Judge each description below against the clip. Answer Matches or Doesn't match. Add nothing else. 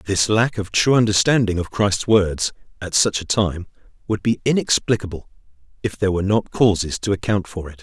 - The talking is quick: Doesn't match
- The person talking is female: Doesn't match